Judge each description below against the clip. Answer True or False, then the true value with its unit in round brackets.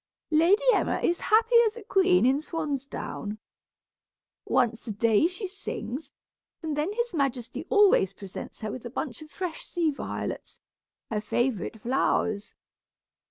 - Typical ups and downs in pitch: False (7.5 semitones)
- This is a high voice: True (290 Hz)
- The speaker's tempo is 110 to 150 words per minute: True (140 wpm)